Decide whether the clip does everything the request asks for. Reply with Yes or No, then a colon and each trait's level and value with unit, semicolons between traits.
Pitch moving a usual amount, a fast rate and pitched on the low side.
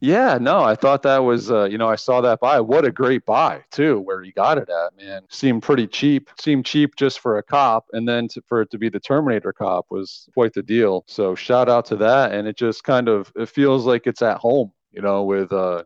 Yes: average, 4.6 semitones; fast, 255 wpm; low, 120 Hz